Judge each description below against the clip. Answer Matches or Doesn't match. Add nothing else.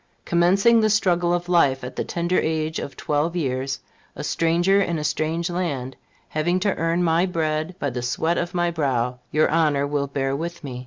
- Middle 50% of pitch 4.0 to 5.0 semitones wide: Doesn't match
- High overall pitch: Doesn't match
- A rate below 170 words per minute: Doesn't match